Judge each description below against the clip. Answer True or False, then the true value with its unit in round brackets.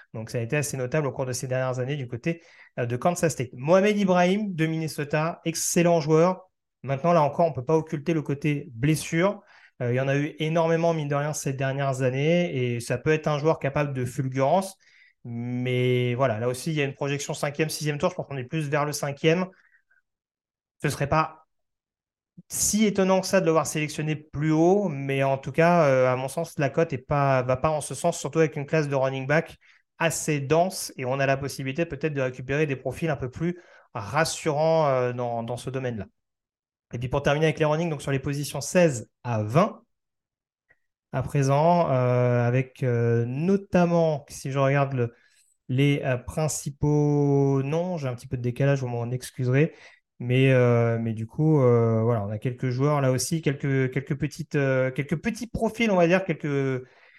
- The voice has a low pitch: False (145 Hz)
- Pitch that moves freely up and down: False (3.7 semitones)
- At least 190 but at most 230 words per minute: True (200 wpm)